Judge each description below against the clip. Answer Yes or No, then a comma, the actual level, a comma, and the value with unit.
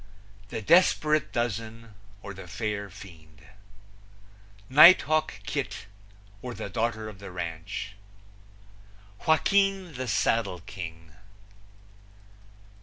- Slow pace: Yes, slow, 90 wpm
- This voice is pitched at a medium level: No, low, 110 Hz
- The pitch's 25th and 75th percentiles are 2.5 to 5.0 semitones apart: No, wide, 5.4 semitones